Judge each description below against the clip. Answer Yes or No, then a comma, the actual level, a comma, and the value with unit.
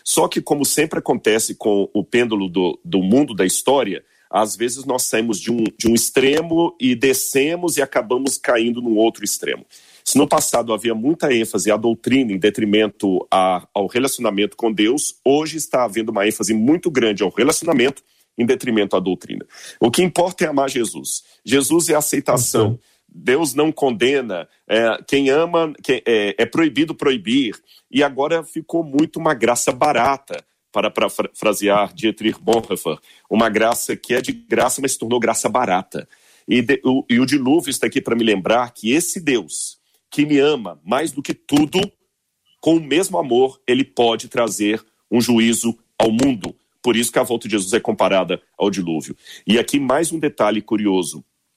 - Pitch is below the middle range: Yes, low, 125 Hz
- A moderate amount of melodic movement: No, wide, 5.8 semitones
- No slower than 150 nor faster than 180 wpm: Yes, average, 175 wpm